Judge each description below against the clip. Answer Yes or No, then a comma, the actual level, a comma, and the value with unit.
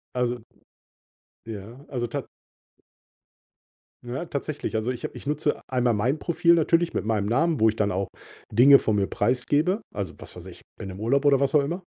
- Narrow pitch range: No, average, 5.1 semitones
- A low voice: Yes, low, 125 Hz